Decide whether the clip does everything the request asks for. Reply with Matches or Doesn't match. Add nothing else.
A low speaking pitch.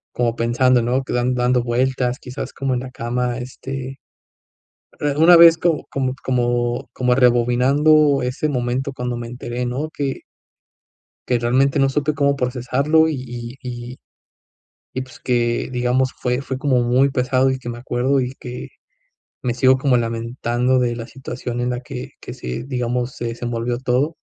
Matches